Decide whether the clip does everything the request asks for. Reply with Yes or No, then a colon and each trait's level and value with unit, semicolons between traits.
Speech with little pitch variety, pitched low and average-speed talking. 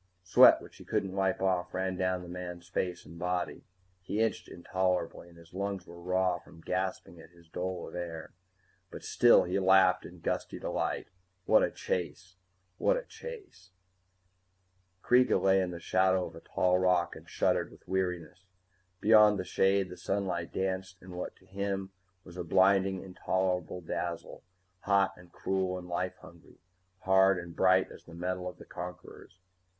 Yes: narrow, 1.3 semitones; very low, 90 Hz; average, 170 wpm